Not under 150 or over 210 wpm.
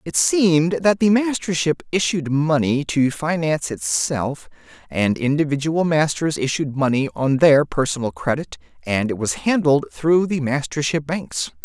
No: average, 140 wpm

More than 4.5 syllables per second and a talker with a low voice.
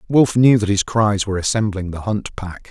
Yes: 5.1 syllables/s; low, 105 Hz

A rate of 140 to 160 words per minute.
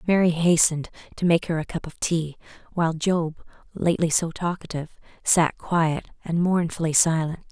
Yes: average, 150 wpm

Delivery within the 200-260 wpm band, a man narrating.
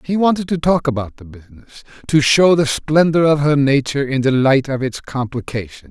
Yes: fast, 205 wpm; male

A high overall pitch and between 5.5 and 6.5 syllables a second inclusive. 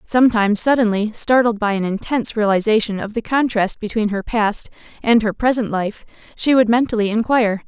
Yes: high, 220 Hz; 5.6 syllables/s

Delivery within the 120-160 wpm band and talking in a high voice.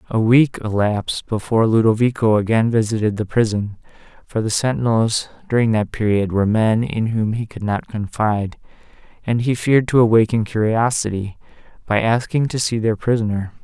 No: average, 155 wpm; low, 110 Hz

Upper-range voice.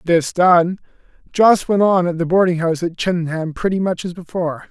No: medium, 175 Hz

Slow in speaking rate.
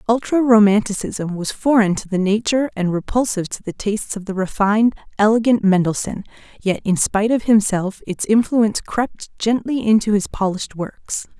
No: average, 160 wpm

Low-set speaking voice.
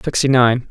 Yes: low, 130 Hz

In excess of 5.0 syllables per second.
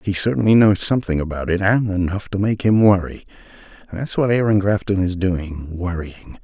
Yes: 5.3 syllables/s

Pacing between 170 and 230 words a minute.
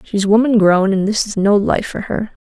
No: fast, 245 wpm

